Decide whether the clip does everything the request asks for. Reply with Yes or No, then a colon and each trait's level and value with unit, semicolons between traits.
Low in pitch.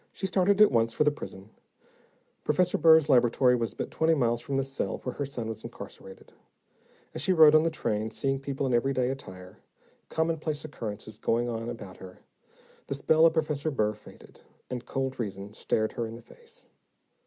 Yes: low, 130 Hz